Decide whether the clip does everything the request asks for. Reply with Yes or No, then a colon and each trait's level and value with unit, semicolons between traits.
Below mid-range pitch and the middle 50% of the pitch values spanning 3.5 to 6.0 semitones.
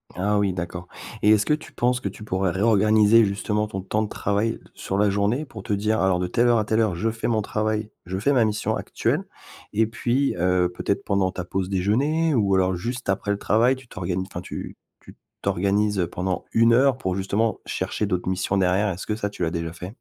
No: low, 105 Hz; average, 3.0 semitones